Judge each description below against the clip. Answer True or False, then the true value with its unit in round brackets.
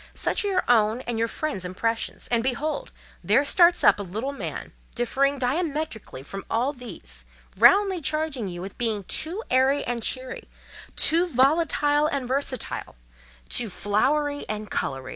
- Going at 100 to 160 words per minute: True (145 wpm)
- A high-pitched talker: True (255 Hz)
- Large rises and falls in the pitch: True (5.8 semitones)